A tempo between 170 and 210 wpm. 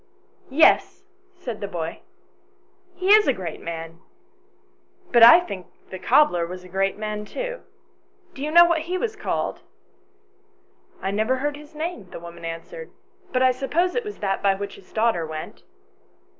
Yes: average, 180 wpm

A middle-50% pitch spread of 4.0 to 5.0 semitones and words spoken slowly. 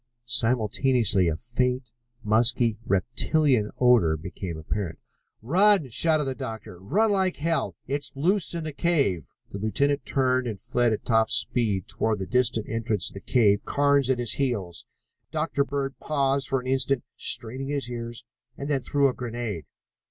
No: average, 4.4 semitones; average, 160 wpm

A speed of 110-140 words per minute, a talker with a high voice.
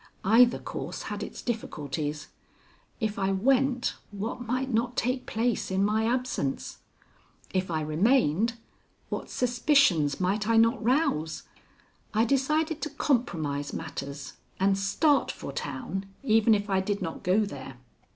Yes: slow, 135 wpm; high, 215 Hz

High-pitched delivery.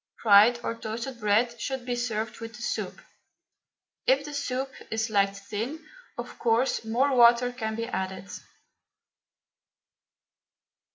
Yes: high, 235 Hz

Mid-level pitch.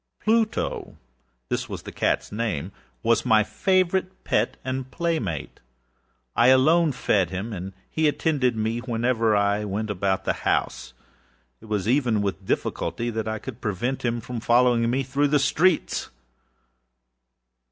No: low, 115 Hz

